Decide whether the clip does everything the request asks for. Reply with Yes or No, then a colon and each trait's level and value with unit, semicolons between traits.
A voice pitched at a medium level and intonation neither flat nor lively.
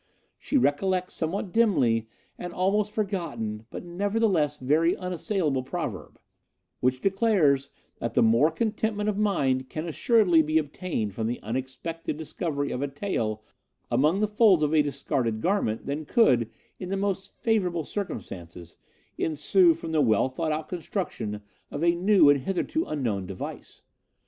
No: medium, 160 Hz; wide, 6.8 semitones